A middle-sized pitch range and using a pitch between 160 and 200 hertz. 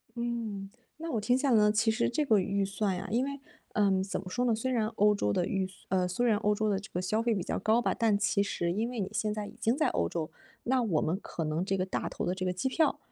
No: average, 3.6 semitones; high, 210 Hz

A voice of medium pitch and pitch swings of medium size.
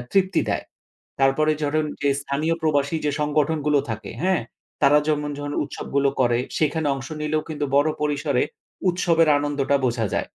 No: medium, 150 Hz; narrow, 1.8 semitones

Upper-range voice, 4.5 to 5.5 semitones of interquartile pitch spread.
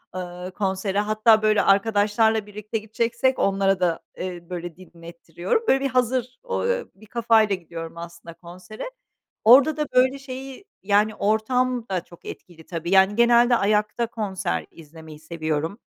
Yes: high, 205 Hz; average, 5.1 semitones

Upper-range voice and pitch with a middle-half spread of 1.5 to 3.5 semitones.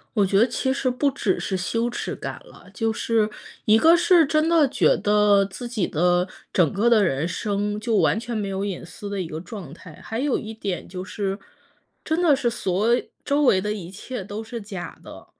No: high, 210 Hz; average, 4.1 semitones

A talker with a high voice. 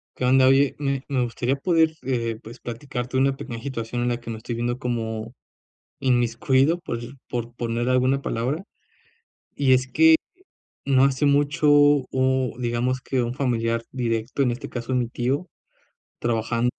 No: low, 125 Hz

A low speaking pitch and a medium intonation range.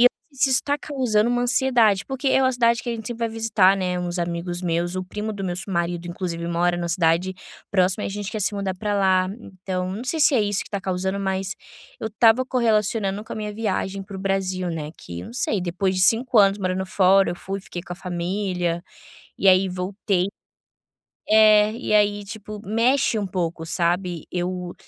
No: high, 195 Hz; average, 3.1 semitones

